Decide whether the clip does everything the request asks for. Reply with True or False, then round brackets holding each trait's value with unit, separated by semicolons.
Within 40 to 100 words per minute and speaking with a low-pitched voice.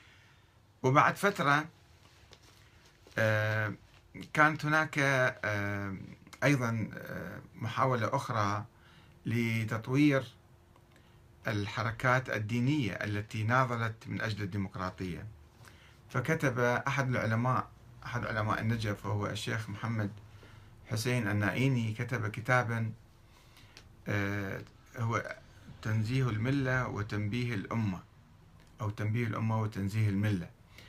True (75 wpm; 110 Hz)